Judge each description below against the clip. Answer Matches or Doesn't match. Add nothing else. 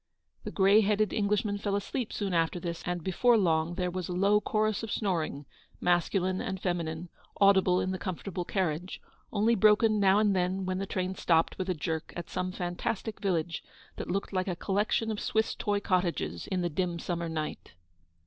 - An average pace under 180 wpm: Doesn't match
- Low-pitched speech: Doesn't match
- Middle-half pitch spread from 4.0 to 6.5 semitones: Doesn't match